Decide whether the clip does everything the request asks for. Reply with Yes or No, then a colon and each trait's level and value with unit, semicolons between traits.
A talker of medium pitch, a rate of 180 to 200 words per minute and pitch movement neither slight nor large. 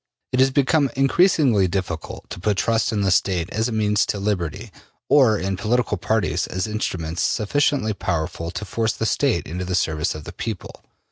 No: low, 105 Hz; average, 185 wpm; average, 4.2 semitones